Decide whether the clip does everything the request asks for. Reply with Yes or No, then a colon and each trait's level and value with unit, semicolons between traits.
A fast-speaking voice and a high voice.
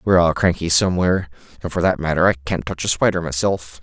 No: fast, 220 wpm; very low, 85 Hz